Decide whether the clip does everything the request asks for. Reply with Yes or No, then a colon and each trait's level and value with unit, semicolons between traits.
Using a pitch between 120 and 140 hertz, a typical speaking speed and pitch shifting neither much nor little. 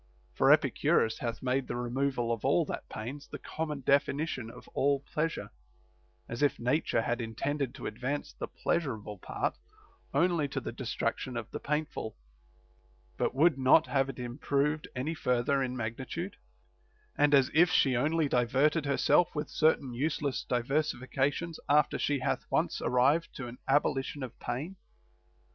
Yes: low, 135 Hz; average, 155 wpm; average, 3.3 semitones